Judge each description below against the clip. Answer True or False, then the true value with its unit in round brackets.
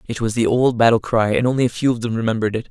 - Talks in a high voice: False (115 Hz)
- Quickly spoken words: True (310 wpm)